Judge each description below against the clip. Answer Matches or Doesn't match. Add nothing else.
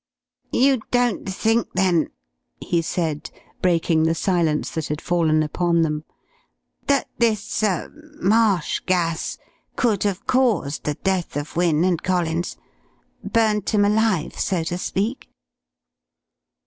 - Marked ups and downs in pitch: Doesn't match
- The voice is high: Doesn't match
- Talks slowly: Matches